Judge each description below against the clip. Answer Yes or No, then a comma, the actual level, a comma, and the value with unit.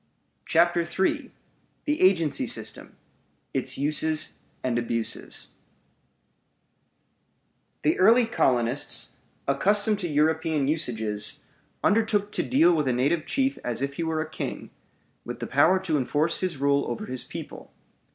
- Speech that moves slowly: Yes, slow, 130 wpm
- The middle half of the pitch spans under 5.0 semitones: No, average, 5.3 semitones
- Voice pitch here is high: No, medium, 155 Hz